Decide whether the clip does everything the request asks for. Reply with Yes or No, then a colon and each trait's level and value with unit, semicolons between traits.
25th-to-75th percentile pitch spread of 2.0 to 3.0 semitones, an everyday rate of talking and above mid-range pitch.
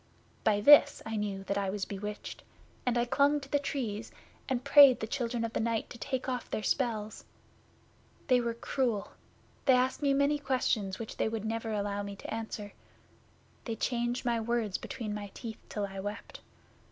No: average, 3.4 semitones; average, 185 wpm; high, 230 Hz